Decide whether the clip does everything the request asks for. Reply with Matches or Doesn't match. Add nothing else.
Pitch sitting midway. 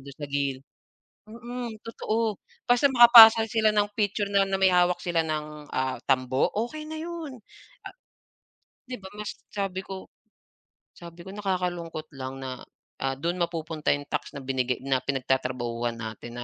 Matches